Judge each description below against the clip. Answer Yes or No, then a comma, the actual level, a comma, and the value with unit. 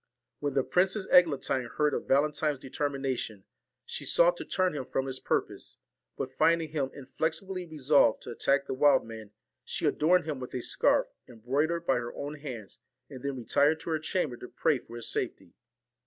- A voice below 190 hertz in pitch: Yes, medium, 140 Hz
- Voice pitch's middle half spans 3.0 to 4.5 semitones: Yes, average, 3.7 semitones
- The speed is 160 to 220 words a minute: Yes, average, 180 wpm